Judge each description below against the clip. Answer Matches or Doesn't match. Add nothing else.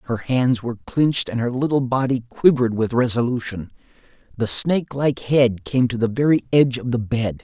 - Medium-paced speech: Matches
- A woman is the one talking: Doesn't match